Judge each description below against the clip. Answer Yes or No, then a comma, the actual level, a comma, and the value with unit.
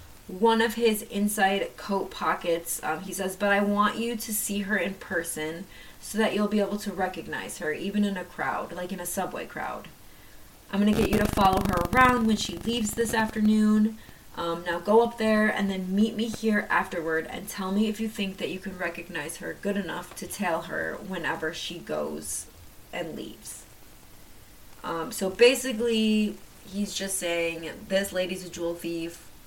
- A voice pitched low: No, high, 195 Hz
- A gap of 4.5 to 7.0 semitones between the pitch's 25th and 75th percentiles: No, average, 3.8 semitones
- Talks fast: No, average, 185 wpm